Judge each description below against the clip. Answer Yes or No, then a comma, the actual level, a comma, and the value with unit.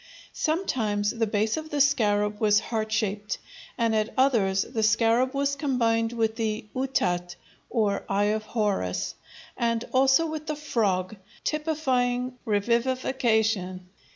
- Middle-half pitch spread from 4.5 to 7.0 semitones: No, average, 3.8 semitones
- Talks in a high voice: Yes, high, 225 Hz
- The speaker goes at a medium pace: No, slow, 125 wpm